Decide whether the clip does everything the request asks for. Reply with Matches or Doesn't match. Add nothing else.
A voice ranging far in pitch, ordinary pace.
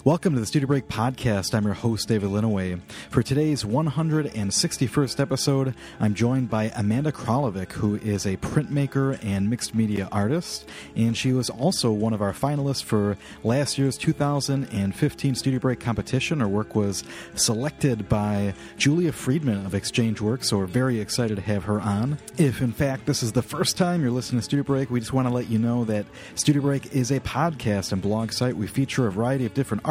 Doesn't match